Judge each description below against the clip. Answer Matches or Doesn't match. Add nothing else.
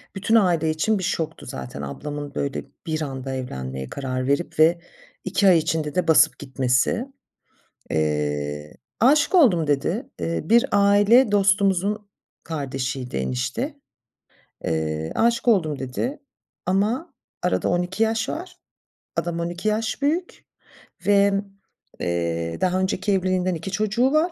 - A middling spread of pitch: Doesn't match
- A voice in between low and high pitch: Matches